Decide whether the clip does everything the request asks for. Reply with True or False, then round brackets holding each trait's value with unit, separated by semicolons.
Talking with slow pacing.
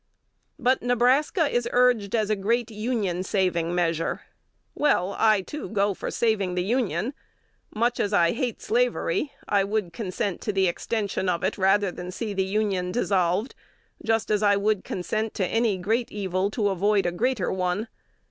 False (165 wpm)